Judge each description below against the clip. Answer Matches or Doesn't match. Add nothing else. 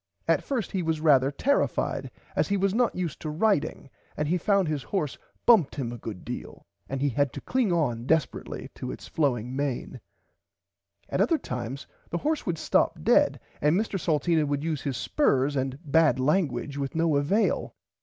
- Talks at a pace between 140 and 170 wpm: Doesn't match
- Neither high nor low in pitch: Matches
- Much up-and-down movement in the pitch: Doesn't match